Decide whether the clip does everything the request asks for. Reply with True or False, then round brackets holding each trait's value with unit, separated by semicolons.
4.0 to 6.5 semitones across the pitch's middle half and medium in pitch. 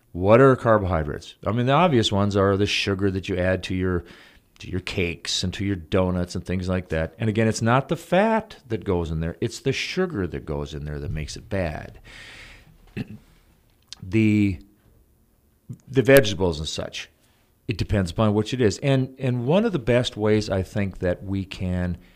False (4.6 semitones; 100 Hz)